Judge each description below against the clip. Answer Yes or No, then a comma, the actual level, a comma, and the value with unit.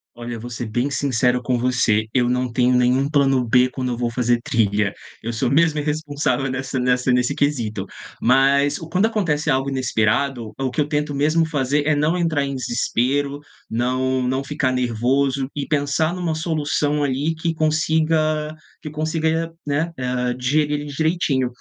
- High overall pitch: No, low, 135 Hz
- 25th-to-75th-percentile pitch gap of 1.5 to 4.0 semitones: Yes, average, 3.3 semitones